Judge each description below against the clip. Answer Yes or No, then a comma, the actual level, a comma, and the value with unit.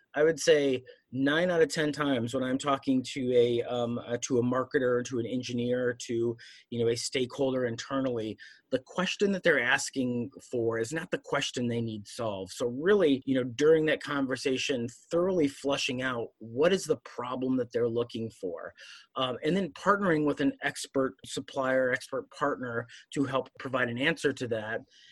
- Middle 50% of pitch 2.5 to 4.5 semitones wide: Yes, average, 2.9 semitones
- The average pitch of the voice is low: Yes, low, 130 Hz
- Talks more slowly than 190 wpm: Yes, average, 180 wpm